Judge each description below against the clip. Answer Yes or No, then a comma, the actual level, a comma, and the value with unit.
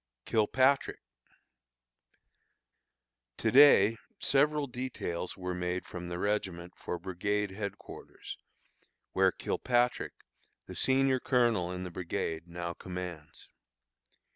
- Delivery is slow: Yes, slow, 95 wpm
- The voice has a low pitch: Yes, very low, 95 Hz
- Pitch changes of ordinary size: No, wide, 5.7 semitones